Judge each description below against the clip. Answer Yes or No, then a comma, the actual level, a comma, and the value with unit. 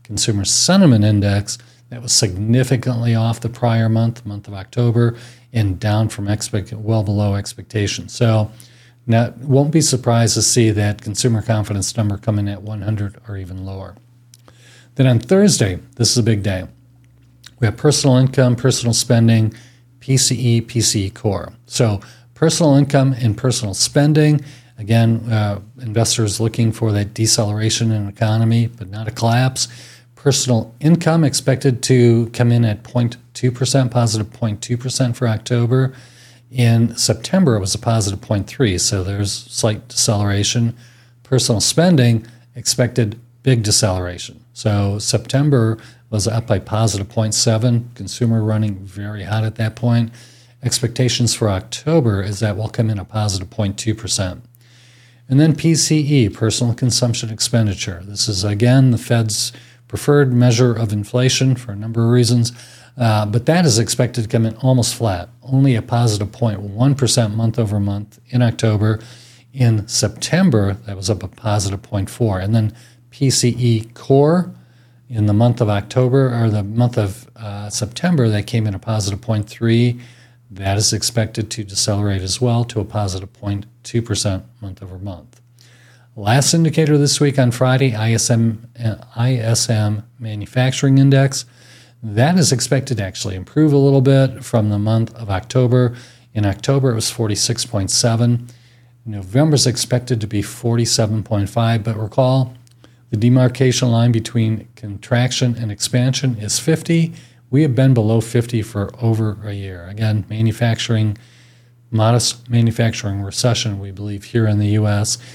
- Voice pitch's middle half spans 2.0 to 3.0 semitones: Yes, narrow, 2.5 semitones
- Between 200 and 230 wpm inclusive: No, average, 145 wpm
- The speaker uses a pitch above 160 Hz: No, low, 115 Hz